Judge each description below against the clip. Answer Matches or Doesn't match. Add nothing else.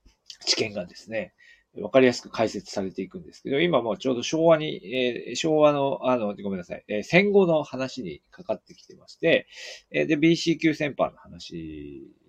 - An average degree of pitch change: Doesn't match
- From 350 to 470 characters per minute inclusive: Matches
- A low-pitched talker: Matches